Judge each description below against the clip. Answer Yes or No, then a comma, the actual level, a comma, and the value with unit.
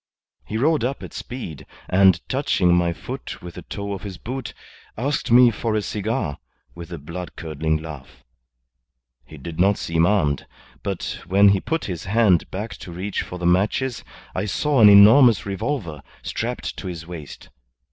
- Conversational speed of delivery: Yes, average, 170 wpm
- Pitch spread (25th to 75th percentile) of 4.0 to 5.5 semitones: Yes, average, 4.7 semitones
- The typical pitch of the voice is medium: No, very low, 95 Hz